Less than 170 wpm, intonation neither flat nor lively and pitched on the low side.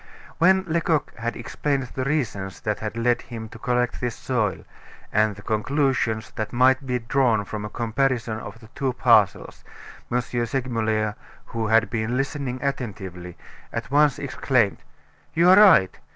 Yes: average, 150 wpm; average, 3.6 semitones; low, 120 Hz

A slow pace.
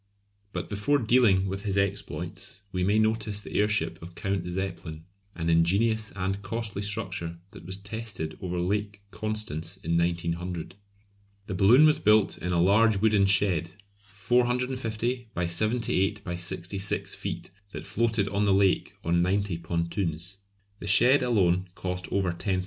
No: average, 150 wpm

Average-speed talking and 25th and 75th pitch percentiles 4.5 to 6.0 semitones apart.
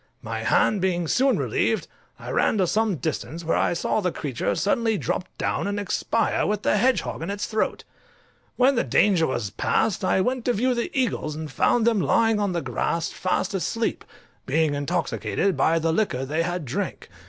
Yes: average, 190 wpm; average, 5.3 semitones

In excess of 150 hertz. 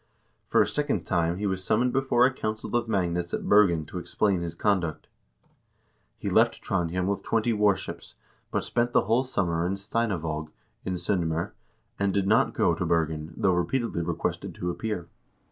No: very low, 95 Hz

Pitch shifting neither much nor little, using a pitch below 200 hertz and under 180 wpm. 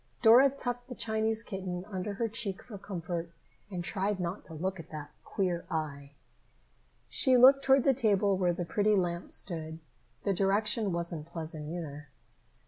Yes: average, 4.3 semitones; high, 190 Hz; average, 160 wpm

